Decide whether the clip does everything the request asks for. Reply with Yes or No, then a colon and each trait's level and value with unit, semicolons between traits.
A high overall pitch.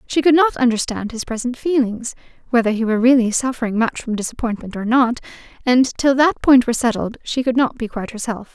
Yes: high, 240 Hz